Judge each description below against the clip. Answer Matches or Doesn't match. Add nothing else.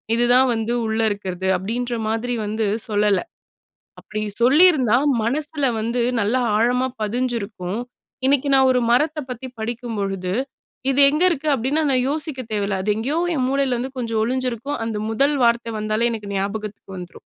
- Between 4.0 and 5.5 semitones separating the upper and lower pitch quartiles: Doesn't match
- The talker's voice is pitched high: Matches